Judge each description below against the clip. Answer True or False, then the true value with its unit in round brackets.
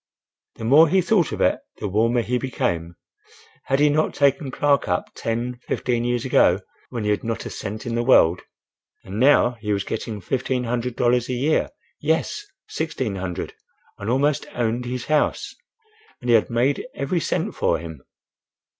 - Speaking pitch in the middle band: False (120 Hz)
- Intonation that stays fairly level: False (3.8 semitones)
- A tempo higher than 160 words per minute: True (170 wpm)